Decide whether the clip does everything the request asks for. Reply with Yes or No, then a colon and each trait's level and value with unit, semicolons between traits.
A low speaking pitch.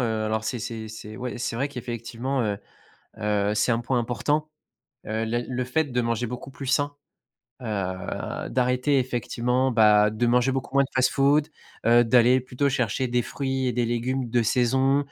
Yes: low, 125 Hz